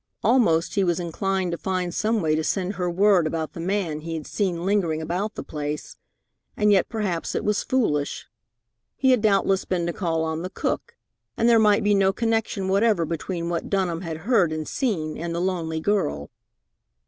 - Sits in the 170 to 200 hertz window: Yes, medium, 185 Hz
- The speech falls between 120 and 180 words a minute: No, average, 195 wpm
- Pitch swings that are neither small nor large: Yes, average, 3.9 semitones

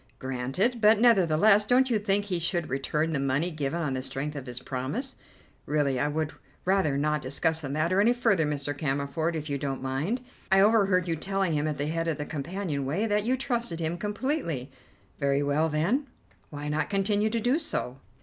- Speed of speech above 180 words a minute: Yes, average, 200 wpm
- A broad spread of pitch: Yes, wide, 6.2 semitones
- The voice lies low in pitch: No, medium, 160 Hz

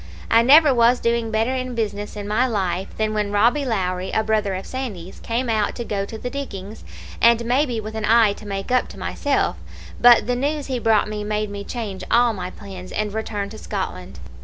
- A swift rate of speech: Yes, fast, 210 wpm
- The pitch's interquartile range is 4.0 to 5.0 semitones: No, average, 3.0 semitones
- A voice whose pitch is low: No, high, 220 Hz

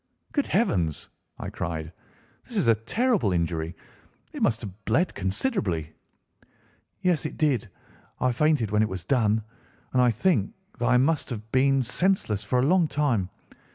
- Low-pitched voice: Yes, low, 115 Hz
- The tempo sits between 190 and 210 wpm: No, average, 155 wpm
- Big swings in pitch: Yes, wide, 7.2 semitones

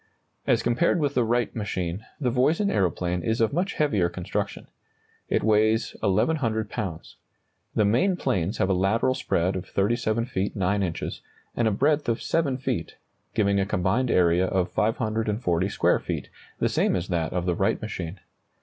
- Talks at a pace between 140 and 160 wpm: No, average, 170 wpm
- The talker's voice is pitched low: Yes, low, 105 Hz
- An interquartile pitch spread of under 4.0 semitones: No, average, 4.4 semitones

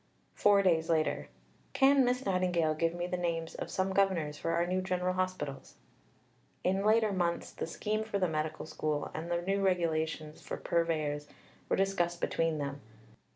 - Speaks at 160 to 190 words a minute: Yes, average, 165 wpm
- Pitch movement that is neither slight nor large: Yes, average, 3.1 semitones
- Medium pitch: Yes, medium, 175 Hz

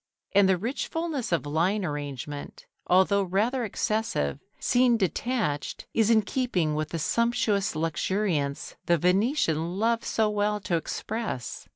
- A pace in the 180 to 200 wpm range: No, slow, 135 wpm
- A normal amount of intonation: No, wide, 5.8 semitones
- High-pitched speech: Yes, high, 195 Hz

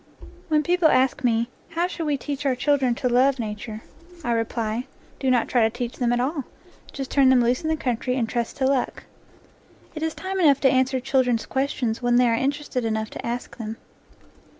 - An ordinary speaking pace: No, fast, 220 wpm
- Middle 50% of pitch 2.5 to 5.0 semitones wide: Yes, average, 2.9 semitones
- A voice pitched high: Yes, very high, 255 Hz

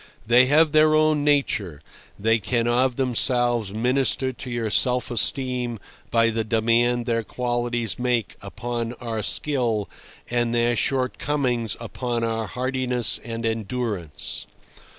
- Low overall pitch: Yes, low, 120 Hz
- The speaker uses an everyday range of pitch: No, narrow, 1.9 semitones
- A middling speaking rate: No, slow, 125 wpm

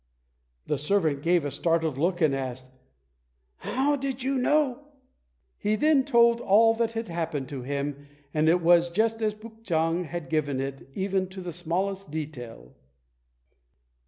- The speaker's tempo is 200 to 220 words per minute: No, average, 155 wpm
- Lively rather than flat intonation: Yes, wide, 7.0 semitones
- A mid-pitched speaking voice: Yes, medium, 175 Hz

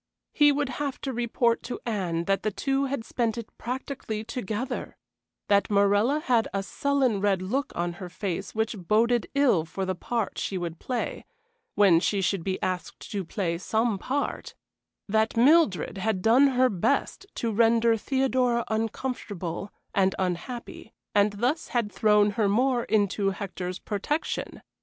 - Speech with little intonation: No, average, 4.2 semitones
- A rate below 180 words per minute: Yes, average, 155 wpm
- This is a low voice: No, high, 220 Hz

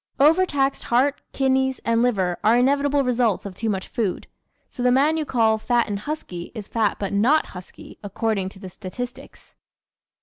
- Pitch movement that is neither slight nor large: Yes, average, 4.9 semitones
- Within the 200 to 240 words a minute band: No, average, 175 wpm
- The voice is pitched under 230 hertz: No, high, 235 Hz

